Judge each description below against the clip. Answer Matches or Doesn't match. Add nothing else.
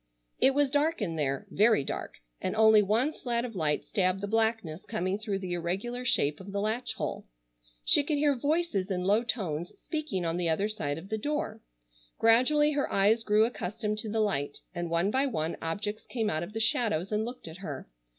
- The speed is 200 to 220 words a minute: Matches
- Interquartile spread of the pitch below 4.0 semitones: Doesn't match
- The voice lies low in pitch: Doesn't match